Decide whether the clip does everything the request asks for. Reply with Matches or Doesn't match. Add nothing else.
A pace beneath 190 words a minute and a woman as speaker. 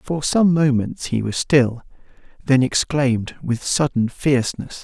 Doesn't match